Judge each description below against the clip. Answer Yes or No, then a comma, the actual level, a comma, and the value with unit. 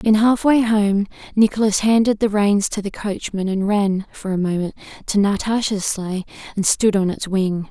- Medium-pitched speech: No, high, 205 Hz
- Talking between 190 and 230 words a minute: No, average, 180 wpm